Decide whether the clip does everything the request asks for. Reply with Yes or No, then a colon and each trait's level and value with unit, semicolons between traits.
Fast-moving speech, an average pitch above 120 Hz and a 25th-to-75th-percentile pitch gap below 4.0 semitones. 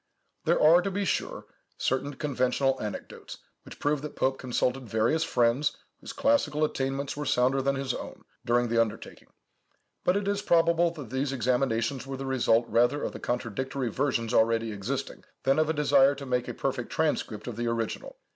No: average, 180 wpm; low, 135 Hz; average, 3.4 semitones